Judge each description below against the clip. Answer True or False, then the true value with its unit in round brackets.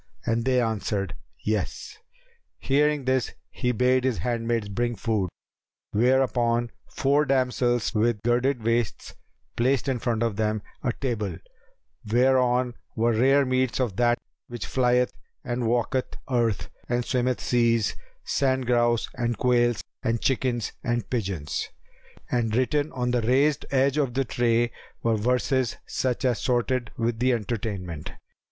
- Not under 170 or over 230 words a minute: False (135 wpm)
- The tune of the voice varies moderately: False (2.0 semitones)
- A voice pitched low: True (120 Hz)